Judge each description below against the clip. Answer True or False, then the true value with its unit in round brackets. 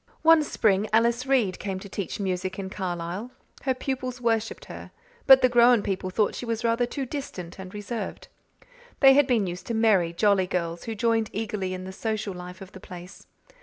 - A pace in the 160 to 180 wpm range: False (195 wpm)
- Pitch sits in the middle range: False (210 Hz)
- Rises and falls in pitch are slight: False (4.3 semitones)